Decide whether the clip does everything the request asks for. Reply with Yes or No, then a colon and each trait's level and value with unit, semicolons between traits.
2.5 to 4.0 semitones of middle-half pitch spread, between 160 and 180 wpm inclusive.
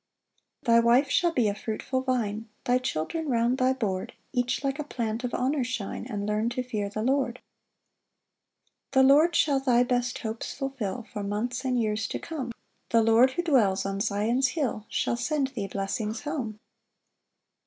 Yes: average, 3.6 semitones; average, 175 wpm